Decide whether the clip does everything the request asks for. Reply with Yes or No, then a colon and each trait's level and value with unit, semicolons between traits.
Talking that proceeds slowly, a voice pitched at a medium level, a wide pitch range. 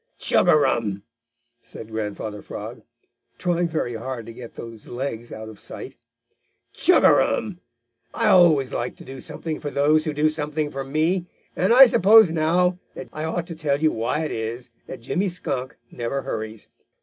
No: average, 175 wpm; medium, 145 Hz; wide, 5.8 semitones